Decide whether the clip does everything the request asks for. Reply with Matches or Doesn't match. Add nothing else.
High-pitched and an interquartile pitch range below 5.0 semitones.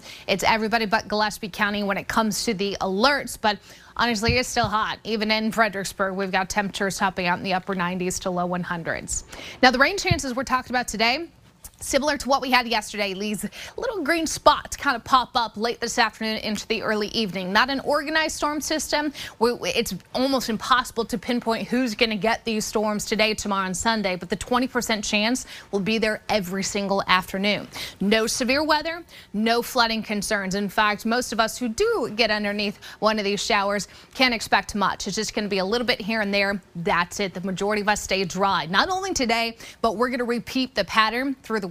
Matches